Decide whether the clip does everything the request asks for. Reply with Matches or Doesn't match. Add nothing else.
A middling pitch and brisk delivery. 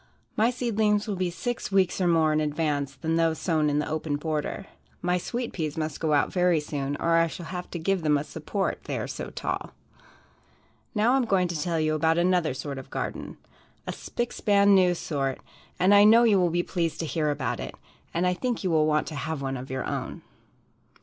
Matches